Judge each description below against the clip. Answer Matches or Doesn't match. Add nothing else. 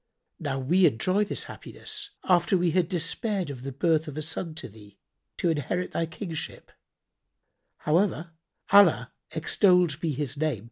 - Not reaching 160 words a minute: Matches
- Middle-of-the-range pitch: Matches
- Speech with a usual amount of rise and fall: Matches